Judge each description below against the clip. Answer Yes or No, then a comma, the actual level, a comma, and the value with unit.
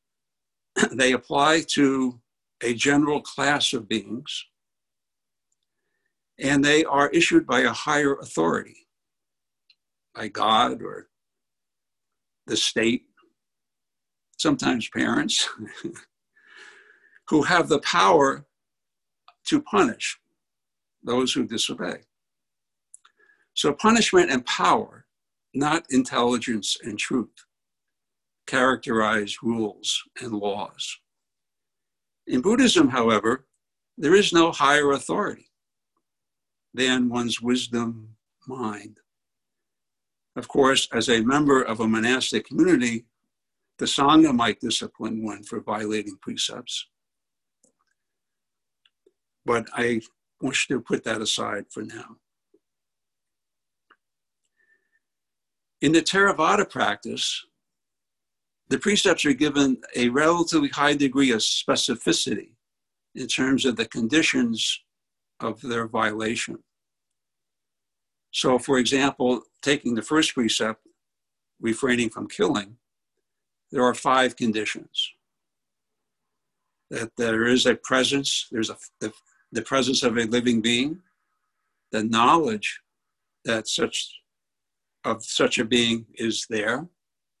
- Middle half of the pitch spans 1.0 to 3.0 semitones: No, average, 4.6 semitones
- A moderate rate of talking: No, slow, 95 wpm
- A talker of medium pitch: No, low, 130 Hz